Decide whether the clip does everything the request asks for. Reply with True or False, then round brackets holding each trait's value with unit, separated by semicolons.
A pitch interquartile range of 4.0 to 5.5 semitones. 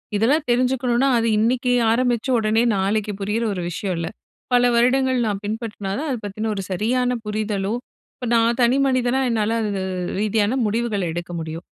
False (3.2 semitones)